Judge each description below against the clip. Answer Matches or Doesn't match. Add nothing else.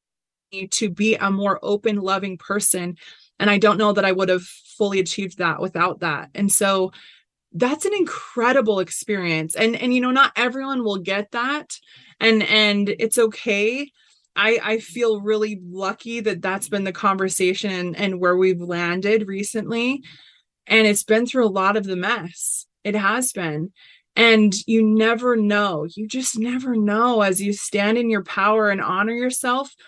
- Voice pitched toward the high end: Matches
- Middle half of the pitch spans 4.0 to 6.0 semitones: Doesn't match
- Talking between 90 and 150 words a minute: Doesn't match